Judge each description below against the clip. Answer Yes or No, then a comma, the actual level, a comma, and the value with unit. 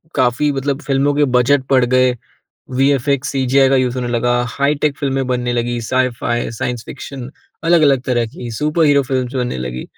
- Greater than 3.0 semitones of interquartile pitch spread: No, narrow, 2.4 semitones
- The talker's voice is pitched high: No, low, 130 Hz